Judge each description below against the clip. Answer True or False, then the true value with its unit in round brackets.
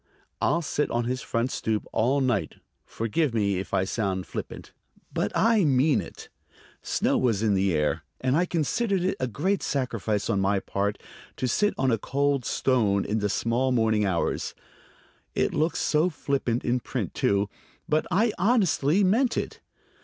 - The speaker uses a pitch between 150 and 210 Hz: False (125 Hz)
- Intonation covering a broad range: True (6.7 semitones)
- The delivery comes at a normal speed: True (165 wpm)